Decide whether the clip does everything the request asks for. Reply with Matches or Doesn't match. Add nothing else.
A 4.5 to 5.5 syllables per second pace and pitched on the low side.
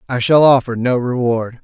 Matches